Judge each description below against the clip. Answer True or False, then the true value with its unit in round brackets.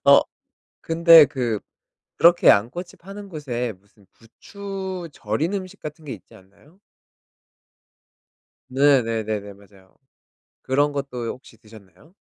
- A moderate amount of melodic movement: False (7.5 semitones)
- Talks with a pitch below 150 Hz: True (135 Hz)